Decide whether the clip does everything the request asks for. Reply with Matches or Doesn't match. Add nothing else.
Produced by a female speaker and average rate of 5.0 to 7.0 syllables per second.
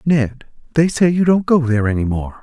Doesn't match